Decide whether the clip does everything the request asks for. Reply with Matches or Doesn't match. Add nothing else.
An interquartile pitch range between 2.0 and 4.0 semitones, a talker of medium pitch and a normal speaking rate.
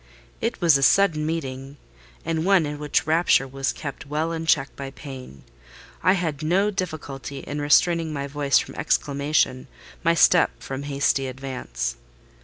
Matches